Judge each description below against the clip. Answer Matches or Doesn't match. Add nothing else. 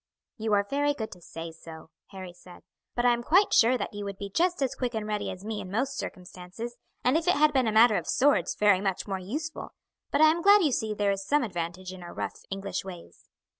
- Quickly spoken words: Matches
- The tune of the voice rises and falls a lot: Matches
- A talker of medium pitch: Doesn't match